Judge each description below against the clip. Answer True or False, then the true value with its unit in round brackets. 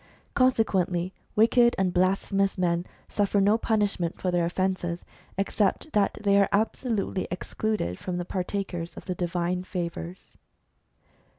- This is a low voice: False (190 Hz)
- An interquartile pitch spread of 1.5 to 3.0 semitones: True (2.5 semitones)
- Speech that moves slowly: True (125 wpm)